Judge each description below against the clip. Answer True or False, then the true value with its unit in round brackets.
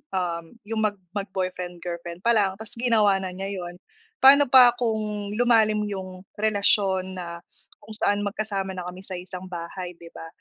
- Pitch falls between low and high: False (195 Hz)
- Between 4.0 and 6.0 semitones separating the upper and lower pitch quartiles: False (2.9 semitones)